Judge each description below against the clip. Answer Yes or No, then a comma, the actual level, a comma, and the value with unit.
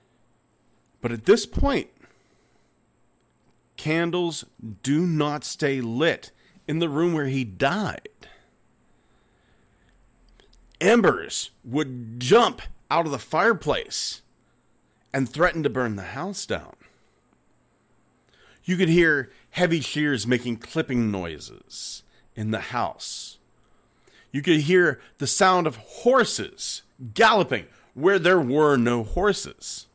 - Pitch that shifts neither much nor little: No, wide, 6.0 semitones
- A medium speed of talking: No, slow, 105 wpm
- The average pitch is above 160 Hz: No, low, 135 Hz